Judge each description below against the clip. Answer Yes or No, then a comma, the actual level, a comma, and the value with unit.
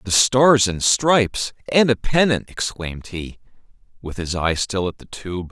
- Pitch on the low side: Yes, low, 110 Hz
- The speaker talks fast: No, average, 175 wpm